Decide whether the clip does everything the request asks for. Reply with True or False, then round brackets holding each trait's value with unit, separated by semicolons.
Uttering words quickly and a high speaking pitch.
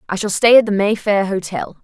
True (230 wpm; 200 Hz)